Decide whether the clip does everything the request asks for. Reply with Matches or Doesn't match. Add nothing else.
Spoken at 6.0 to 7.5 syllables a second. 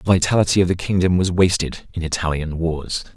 Doesn't match